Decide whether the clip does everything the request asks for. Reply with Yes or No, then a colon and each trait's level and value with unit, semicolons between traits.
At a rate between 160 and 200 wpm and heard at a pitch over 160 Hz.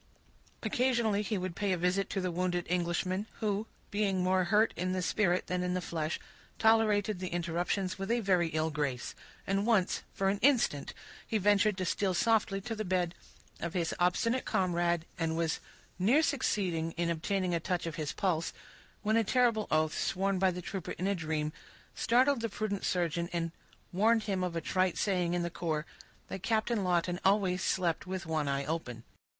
Yes: average, 185 wpm; medium, 185 Hz